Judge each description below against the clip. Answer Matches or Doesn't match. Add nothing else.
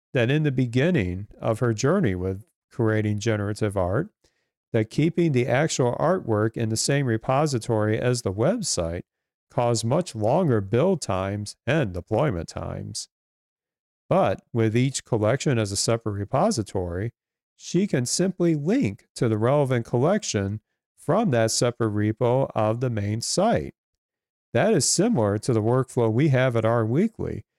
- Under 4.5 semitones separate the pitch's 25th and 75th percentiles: Matches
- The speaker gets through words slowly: Doesn't match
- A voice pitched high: Doesn't match